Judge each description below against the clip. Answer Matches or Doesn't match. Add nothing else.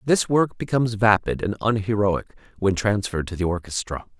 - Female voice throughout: Doesn't match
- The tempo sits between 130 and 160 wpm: Matches